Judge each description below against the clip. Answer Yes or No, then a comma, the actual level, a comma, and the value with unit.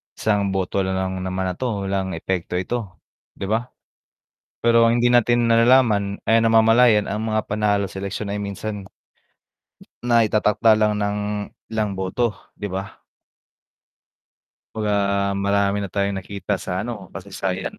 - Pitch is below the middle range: Yes, low, 100 Hz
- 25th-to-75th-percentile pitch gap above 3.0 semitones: No, narrow, 2.5 semitones